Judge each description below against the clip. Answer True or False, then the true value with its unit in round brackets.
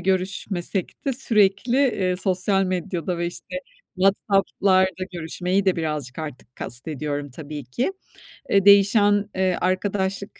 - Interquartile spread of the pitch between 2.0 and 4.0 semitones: True (2.9 semitones)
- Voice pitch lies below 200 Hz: True (185 Hz)